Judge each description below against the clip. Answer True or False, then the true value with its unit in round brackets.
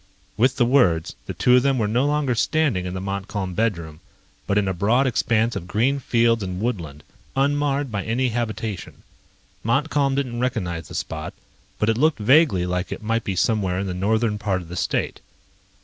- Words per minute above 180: True (190 wpm)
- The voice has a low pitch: True (110 Hz)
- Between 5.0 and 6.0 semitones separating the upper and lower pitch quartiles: True (5.4 semitones)